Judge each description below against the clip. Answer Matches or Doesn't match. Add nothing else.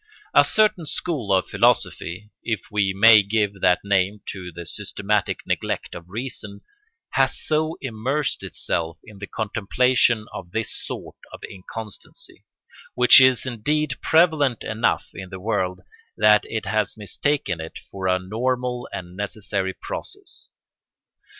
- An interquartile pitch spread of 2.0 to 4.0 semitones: Doesn't match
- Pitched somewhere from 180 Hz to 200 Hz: Doesn't match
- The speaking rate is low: Matches